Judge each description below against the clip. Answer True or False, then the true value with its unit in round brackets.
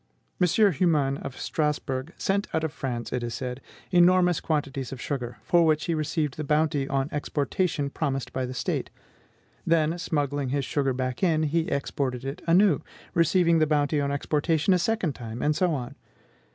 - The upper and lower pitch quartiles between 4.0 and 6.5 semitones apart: False (3.5 semitones)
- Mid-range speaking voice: True (150 Hz)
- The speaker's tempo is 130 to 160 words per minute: False (175 wpm)